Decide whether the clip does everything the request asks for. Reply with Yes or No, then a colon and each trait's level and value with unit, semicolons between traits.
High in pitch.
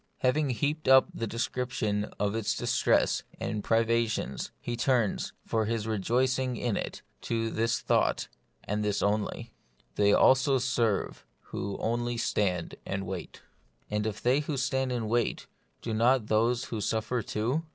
No: low, 115 Hz